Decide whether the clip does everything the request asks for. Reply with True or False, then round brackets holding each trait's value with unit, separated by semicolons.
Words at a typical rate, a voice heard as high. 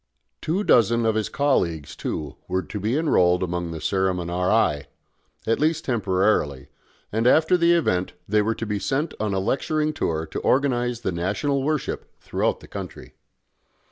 False (160 wpm; 110 Hz)